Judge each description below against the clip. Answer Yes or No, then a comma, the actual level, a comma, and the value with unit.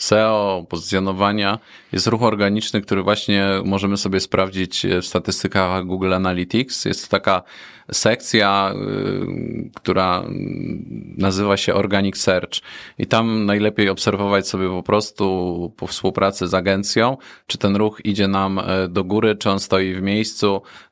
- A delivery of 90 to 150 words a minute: Yes, average, 130 wpm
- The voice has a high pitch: No, low, 100 Hz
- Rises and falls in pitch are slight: Yes, narrow, 1.9 semitones